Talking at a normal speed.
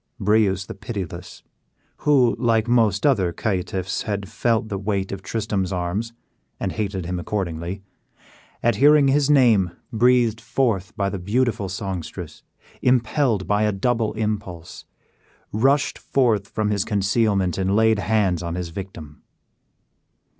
No: slow, 130 wpm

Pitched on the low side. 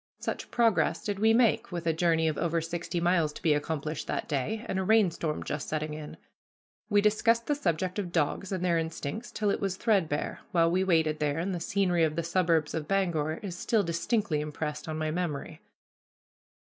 No: medium, 170 Hz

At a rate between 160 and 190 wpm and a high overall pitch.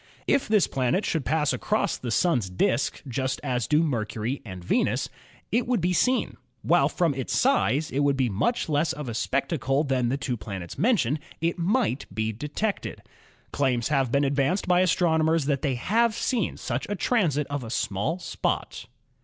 No: average, 185 wpm; medium, 145 Hz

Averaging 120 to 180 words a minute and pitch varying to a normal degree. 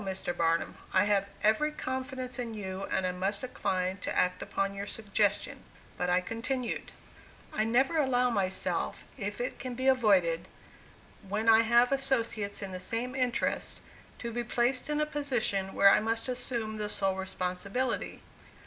Yes: average, 160 wpm; average, 4.4 semitones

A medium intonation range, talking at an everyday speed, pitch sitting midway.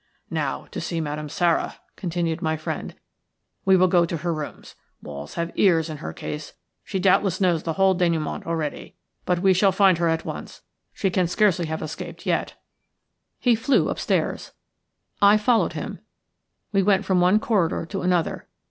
Yes: average, 3.0 semitones; average, 170 wpm; medium, 175 Hz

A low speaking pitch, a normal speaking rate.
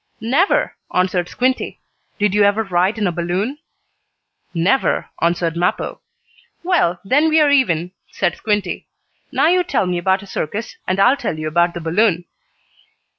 No: high, 190 Hz; average, 155 wpm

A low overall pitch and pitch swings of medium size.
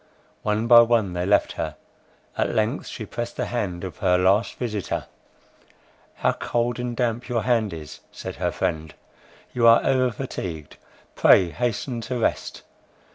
Yes: low, 115 Hz; average, 4.2 semitones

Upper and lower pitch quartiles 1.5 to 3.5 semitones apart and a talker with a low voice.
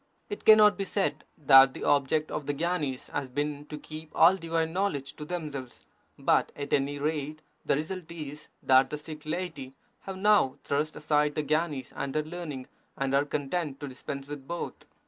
No: average, 2.8 semitones; medium, 150 Hz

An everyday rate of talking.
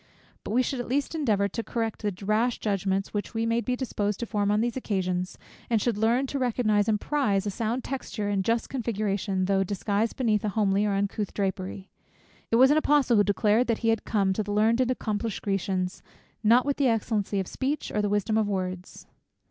No: fast, 215 wpm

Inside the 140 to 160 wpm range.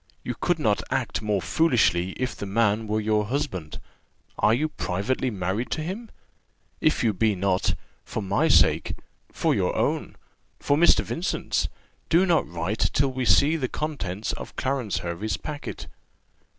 Yes: average, 155 wpm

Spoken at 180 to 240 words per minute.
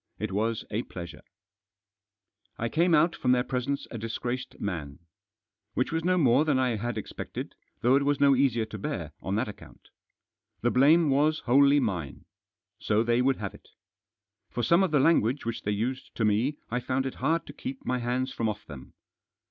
Yes: average, 190 wpm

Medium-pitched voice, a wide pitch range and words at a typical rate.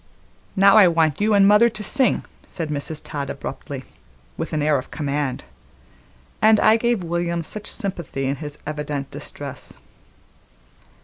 Yes: medium, 165 Hz; wide, 5.9 semitones; average, 145 wpm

